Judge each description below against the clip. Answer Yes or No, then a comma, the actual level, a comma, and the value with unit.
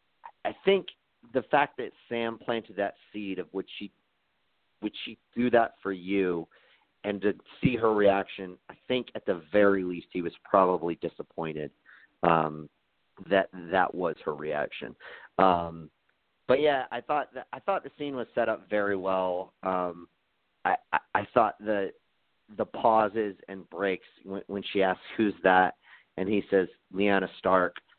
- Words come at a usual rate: Yes, average, 160 wpm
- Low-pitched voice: Yes, very low, 95 Hz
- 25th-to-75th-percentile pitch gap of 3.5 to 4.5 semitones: No, narrow, 2.4 semitones